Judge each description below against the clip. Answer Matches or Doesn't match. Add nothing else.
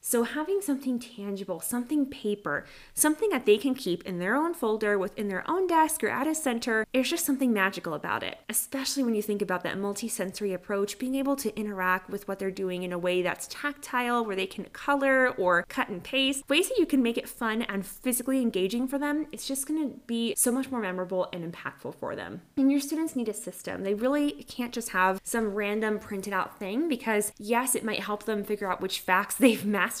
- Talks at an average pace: Doesn't match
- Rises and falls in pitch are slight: Doesn't match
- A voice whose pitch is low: Doesn't match